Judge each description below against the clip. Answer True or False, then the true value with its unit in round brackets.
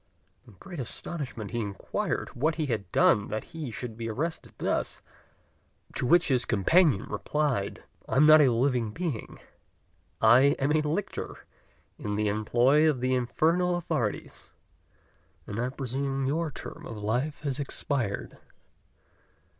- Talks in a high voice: False (130 Hz)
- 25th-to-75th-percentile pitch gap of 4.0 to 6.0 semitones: True (5.2 semitones)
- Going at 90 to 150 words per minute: True (140 wpm)